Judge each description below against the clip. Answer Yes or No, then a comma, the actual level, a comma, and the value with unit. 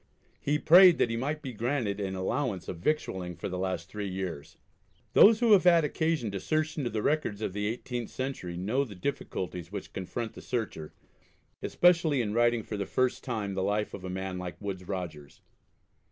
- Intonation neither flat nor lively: No, wide, 7.0 semitones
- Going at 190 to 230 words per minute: Yes, average, 195 wpm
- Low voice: Yes, low, 105 Hz